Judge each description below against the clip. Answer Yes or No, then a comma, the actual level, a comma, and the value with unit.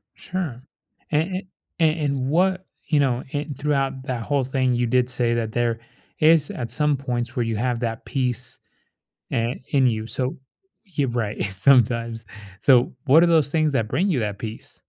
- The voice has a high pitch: No, low, 130 Hz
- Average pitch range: Yes, average, 3.7 semitones